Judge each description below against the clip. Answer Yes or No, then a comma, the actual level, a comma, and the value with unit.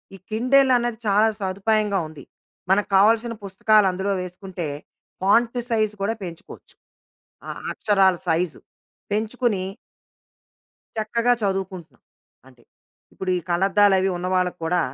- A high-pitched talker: Yes, high, 195 Hz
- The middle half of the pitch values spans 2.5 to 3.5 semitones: Yes, average, 3.1 semitones